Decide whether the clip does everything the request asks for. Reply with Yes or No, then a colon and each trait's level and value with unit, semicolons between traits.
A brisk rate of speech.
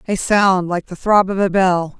Yes: fast, 240 wpm